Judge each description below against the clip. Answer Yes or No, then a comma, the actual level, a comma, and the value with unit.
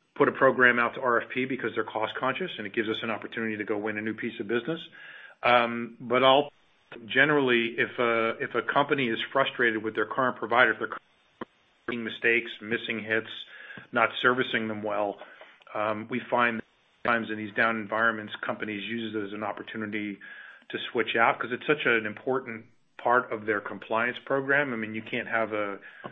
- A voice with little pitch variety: Yes, narrow, 2.3 semitones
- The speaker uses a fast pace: No, average, 190 wpm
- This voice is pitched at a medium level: No, low, 115 Hz